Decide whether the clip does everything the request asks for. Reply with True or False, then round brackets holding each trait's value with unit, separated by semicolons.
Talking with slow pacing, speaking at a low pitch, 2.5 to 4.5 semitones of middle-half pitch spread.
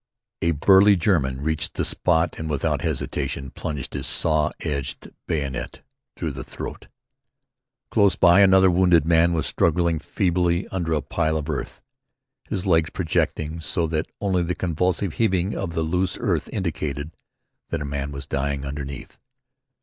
False (150 wpm; 80 Hz; 3.4 semitones)